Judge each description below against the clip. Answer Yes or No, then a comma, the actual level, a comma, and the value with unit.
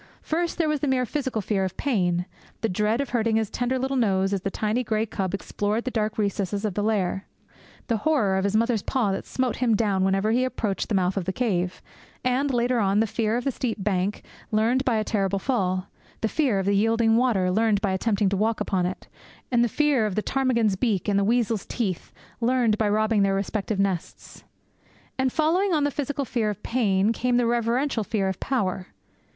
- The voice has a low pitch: No, high, 220 Hz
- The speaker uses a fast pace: Yes, fast, 215 wpm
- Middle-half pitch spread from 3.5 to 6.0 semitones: Yes, average, 3.9 semitones